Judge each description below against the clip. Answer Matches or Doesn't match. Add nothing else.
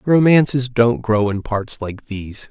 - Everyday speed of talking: Matches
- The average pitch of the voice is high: Doesn't match